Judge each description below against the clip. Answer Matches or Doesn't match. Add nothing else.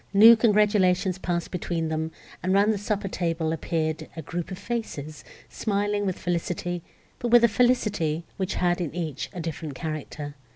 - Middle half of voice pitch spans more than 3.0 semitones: Matches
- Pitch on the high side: Doesn't match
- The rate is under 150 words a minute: Doesn't match